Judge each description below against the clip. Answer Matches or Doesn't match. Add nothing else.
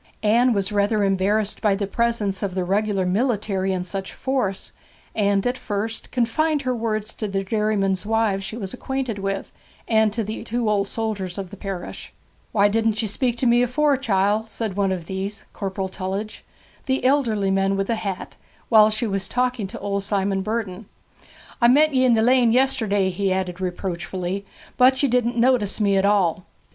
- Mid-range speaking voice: Doesn't match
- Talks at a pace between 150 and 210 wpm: Matches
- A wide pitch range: Doesn't match